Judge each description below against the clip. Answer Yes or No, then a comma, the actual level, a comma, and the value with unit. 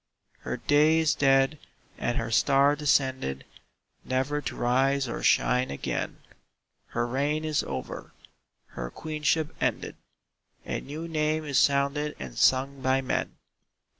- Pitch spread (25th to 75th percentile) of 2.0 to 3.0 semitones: Yes, narrow, 2.5 semitones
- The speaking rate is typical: No, slow, 130 wpm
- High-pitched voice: No, medium, 140 Hz